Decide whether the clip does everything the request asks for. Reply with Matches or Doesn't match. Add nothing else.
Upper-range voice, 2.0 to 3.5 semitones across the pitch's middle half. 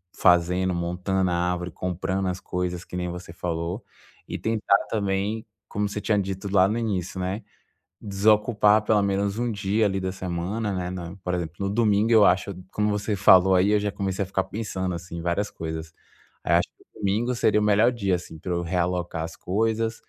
Doesn't match